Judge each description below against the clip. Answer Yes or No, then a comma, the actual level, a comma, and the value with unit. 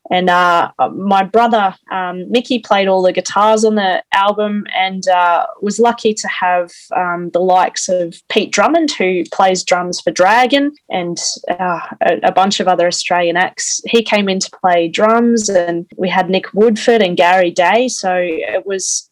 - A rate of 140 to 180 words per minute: Yes, average, 175 wpm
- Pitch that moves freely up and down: No, average, 3.1 semitones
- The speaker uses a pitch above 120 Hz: Yes, high, 190 Hz